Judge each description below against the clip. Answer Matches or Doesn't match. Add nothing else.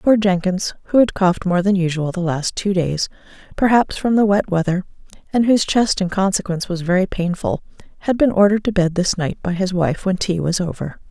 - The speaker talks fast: Matches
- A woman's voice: Matches